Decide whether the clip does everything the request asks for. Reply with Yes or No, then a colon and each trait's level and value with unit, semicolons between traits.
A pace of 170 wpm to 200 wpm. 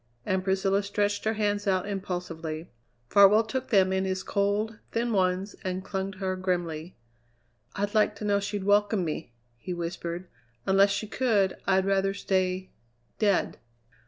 No: average, 155 wpm